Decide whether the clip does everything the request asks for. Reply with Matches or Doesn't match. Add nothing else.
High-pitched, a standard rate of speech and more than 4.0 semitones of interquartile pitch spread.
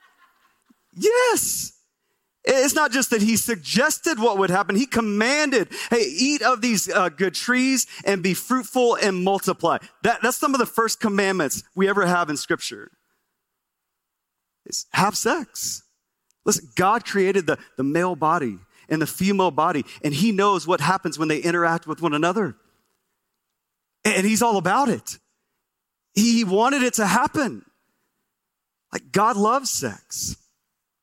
Matches